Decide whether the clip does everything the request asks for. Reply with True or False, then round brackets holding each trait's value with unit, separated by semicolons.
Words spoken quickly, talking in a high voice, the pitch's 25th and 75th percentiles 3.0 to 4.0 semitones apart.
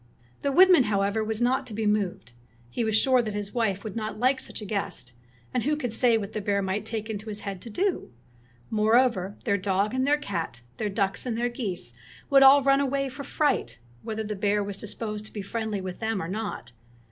True (225 wpm; 215 Hz; 3.5 semitones)